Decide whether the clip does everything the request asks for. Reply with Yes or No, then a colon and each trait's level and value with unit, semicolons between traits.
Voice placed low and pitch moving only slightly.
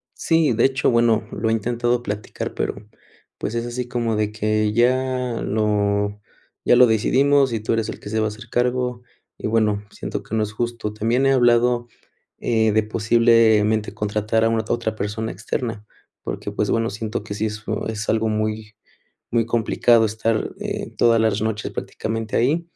Yes: low, 110 Hz; narrow, 1.9 semitones